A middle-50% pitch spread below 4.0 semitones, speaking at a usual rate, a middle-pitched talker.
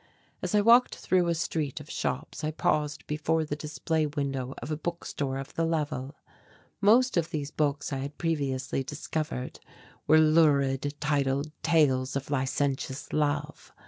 Yes: narrow, 2.5 semitones; average, 150 wpm; medium, 150 Hz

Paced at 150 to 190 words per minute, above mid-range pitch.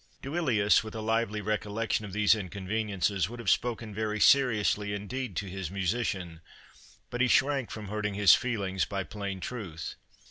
No: average, 155 wpm; low, 105 Hz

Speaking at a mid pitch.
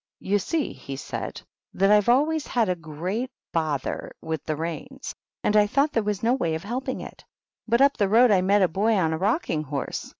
No: high, 205 Hz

